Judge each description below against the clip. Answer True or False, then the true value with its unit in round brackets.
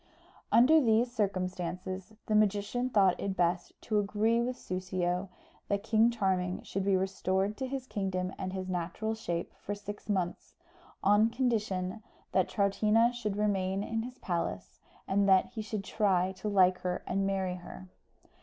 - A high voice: True (195 Hz)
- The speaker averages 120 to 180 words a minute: True (155 wpm)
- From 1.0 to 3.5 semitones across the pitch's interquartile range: True (2.8 semitones)